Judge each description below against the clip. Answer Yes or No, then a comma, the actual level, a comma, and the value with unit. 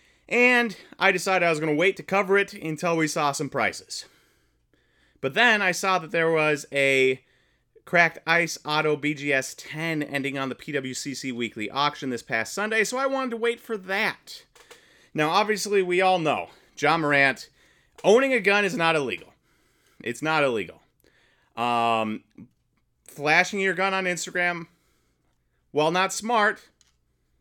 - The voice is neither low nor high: Yes, medium, 165 Hz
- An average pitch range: No, wide, 6.1 semitones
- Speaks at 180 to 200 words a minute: No, average, 155 wpm